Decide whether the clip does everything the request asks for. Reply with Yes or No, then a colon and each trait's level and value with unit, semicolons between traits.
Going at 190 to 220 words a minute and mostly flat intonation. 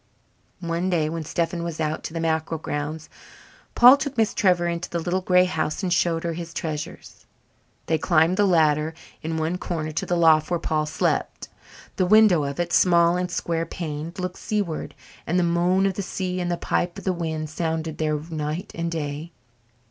Yes: average, 195 wpm; narrow, 2.3 semitones